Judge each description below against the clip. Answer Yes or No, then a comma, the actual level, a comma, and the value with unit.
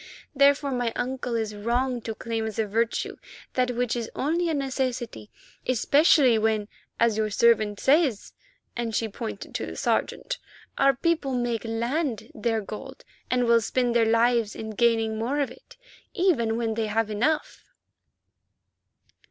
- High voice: Yes, high, 235 Hz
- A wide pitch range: No, average, 3.0 semitones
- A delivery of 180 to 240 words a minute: No, average, 150 wpm